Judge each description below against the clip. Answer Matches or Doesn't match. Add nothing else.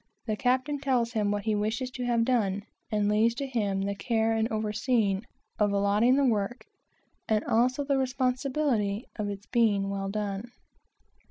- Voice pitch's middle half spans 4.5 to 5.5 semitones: Doesn't match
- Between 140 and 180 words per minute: Matches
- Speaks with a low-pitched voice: Doesn't match